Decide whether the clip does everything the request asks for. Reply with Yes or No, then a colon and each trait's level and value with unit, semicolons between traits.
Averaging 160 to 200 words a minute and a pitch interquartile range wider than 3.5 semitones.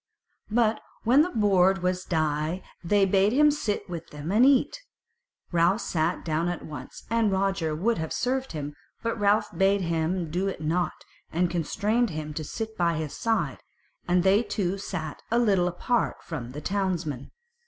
Yes: average, 175 wpm; average, 4.7 semitones